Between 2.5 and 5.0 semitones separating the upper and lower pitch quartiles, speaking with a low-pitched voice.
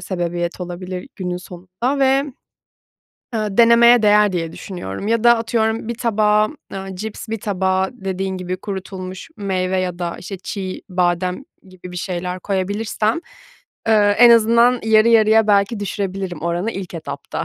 No: average, 3.3 semitones; high, 195 Hz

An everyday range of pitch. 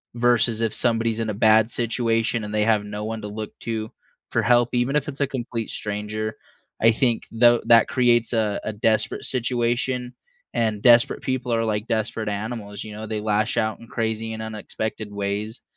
No: narrow, 1.8 semitones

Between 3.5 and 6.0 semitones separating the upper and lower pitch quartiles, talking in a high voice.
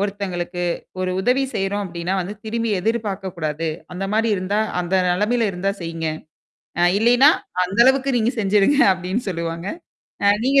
Yes: average, 4.0 semitones; high, 195 Hz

